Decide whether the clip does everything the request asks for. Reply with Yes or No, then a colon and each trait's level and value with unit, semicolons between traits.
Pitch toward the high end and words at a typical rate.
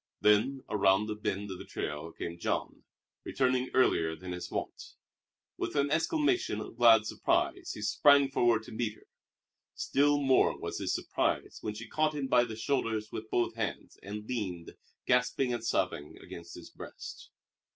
No: low, 110 Hz; average, 165 wpm